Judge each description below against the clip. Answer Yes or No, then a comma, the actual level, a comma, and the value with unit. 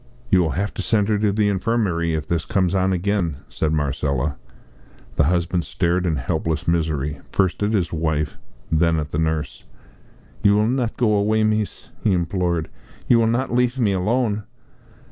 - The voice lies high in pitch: No, very low, 90 Hz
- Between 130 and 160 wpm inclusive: No, average, 175 wpm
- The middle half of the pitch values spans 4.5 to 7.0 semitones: Yes, average, 4.9 semitones